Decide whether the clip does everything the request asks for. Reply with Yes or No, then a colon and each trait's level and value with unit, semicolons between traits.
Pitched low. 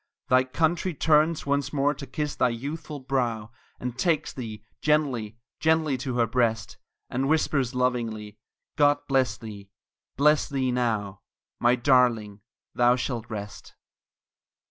Yes: low, 125 Hz